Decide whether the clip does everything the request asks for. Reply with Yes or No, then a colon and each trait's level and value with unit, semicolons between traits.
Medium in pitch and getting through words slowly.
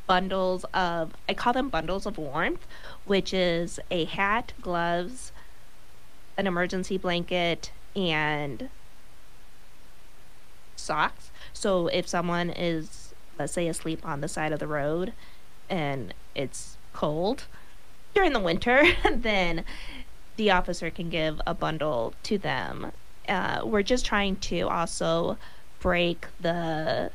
Yes: medium, 175 Hz; slow, 120 wpm